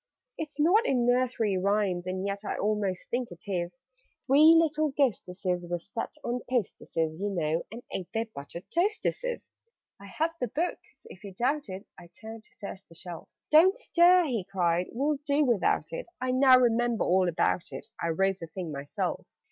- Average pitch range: No, wide, 7.4 semitones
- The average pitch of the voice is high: Yes, high, 220 Hz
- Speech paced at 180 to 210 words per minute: Yes, average, 190 wpm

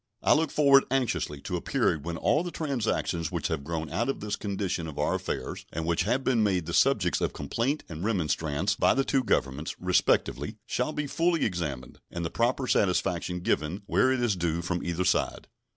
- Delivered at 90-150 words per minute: No, average, 200 wpm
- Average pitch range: No, wide, 7.6 semitones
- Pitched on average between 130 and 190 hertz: No, very low, 90 Hz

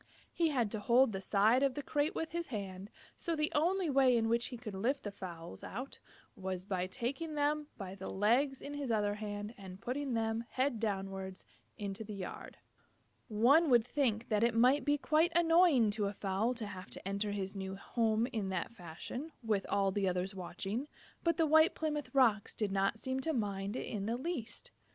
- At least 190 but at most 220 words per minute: Yes, average, 200 wpm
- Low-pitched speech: No, high, 225 Hz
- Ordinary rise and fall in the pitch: No, wide, 5.8 semitones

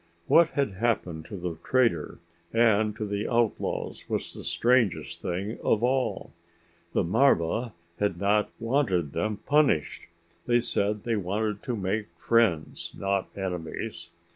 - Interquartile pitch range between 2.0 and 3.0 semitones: No, average, 4.0 semitones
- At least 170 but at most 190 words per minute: No, slow, 135 wpm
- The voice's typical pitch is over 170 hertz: No, low, 105 Hz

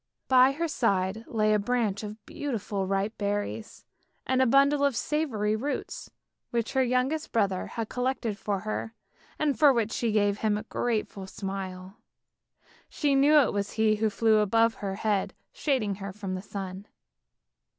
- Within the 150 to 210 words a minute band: Yes, average, 160 wpm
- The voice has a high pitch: Yes, high, 220 Hz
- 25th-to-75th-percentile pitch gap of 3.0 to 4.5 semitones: Yes, average, 3.9 semitones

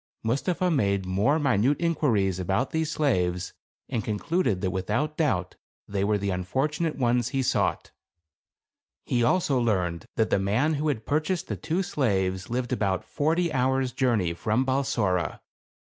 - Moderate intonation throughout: No, wide, 7.2 semitones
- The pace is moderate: Yes, average, 145 wpm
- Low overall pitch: Yes, low, 120 Hz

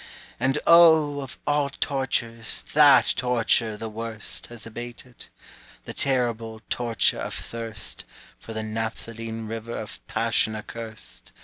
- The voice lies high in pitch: No, low, 115 Hz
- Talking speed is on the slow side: Yes, slow, 120 wpm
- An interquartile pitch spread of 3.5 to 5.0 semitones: No, average, 3.0 semitones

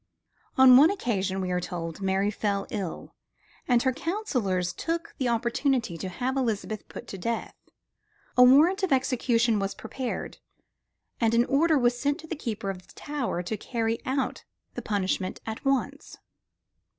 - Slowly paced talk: No, average, 165 wpm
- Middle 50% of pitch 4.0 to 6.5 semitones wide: Yes, average, 5.3 semitones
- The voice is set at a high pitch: Yes, high, 235 Hz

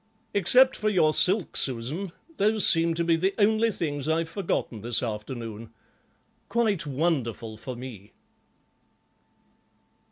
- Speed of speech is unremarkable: No, slow, 120 wpm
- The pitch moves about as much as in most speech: No, wide, 8.7 semitones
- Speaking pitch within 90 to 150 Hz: No, medium, 160 Hz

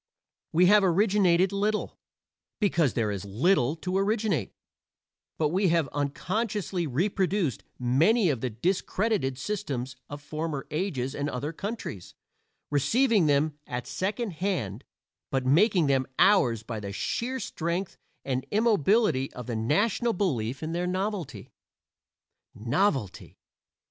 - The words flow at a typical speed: No, slow, 125 wpm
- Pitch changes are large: Yes, wide, 7.2 semitones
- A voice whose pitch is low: No, medium, 165 Hz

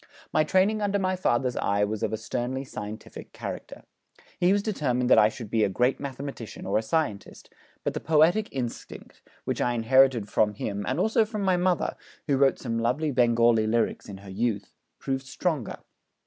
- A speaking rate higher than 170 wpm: Yes, average, 185 wpm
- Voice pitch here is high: No, low, 125 Hz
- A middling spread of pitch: No, wide, 6.2 semitones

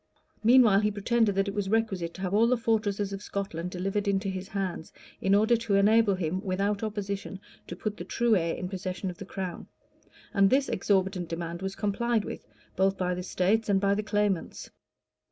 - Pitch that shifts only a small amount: Yes, narrow, 2.2 semitones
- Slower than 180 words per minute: No, average, 195 wpm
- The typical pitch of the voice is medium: No, high, 195 Hz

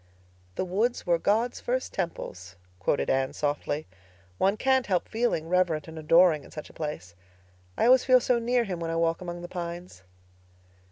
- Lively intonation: Yes, wide, 6.4 semitones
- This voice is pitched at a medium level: Yes, medium, 175 Hz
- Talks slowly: No, average, 175 wpm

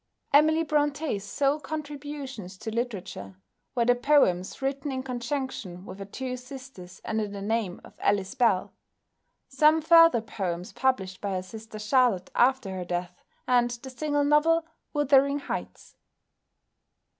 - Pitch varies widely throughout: Yes, wide, 6.3 semitones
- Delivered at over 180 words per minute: No, slow, 135 wpm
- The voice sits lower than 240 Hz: No, very high, 250 Hz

